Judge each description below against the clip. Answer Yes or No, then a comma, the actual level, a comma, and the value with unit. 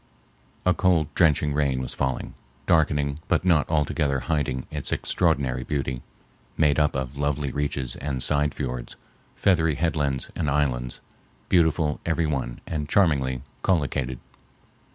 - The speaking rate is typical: No, slow, 130 wpm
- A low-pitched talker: Yes, very low, 70 Hz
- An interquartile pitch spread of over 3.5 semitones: No, average, 2.9 semitones